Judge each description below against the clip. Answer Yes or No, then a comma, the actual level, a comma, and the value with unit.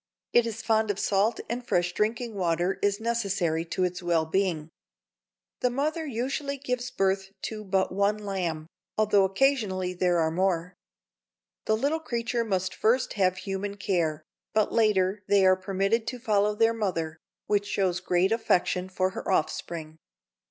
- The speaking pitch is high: Yes, high, 195 Hz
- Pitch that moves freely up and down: No, average, 3.7 semitones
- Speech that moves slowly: No, average, 155 wpm